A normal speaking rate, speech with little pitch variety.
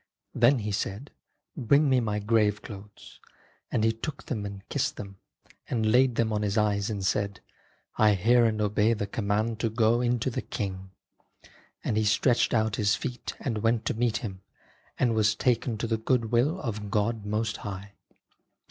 Yes: average, 185 wpm; narrow, 2.3 semitones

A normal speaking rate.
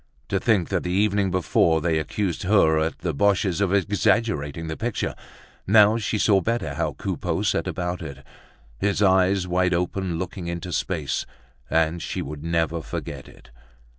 Yes: average, 165 wpm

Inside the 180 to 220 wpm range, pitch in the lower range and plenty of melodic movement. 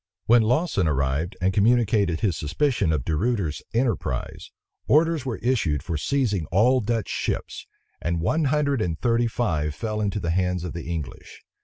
No: average, 165 wpm; low, 100 Hz; wide, 6.6 semitones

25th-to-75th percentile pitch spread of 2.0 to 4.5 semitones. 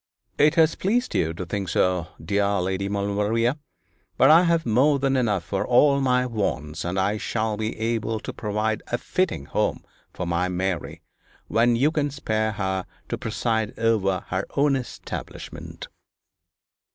No: average, 5.2 semitones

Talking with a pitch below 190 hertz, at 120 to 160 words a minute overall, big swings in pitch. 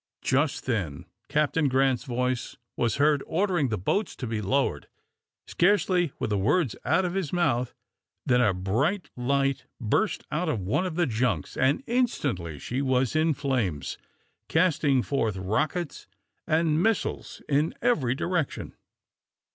Yes: medium, 140 Hz; average, 140 wpm; wide, 5.7 semitones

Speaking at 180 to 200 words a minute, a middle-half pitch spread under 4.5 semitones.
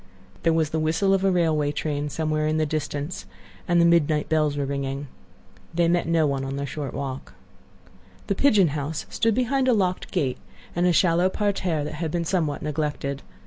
Yes: average, 190 wpm; average, 3.3 semitones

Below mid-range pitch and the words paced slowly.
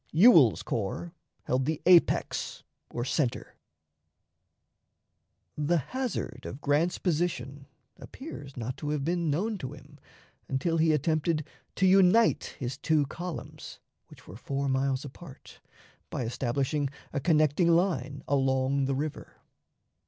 No: medium, 145 Hz; slow, 125 wpm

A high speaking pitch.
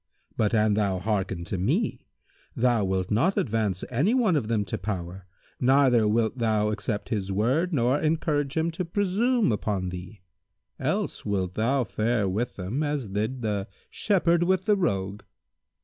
No: low, 110 Hz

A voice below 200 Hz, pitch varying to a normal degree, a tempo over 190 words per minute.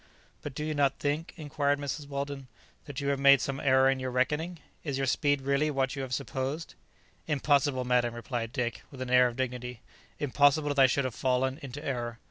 No: low, 135 Hz; narrow, 2.0 semitones; fast, 205 wpm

